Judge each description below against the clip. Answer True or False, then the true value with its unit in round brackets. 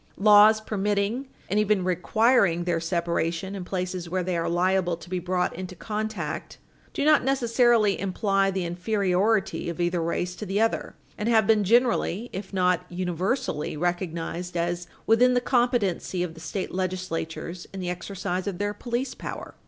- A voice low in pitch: False (185 Hz)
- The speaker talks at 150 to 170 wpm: True (160 wpm)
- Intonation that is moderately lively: True (3.4 semitones)